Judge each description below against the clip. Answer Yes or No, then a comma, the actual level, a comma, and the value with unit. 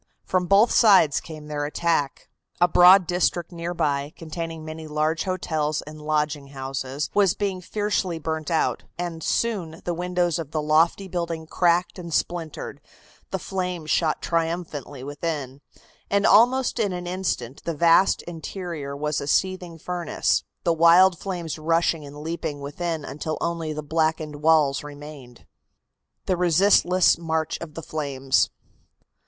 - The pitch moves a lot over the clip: No, average, 2.9 semitones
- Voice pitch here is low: No, medium, 165 Hz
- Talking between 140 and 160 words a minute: Yes, average, 145 wpm